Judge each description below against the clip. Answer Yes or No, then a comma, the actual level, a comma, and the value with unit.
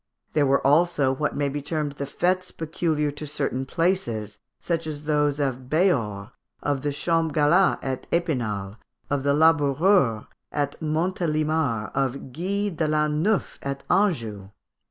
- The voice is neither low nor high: Yes, medium, 150 Hz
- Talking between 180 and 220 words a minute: No, average, 140 wpm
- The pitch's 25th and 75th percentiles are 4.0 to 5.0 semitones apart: No, average, 3.4 semitones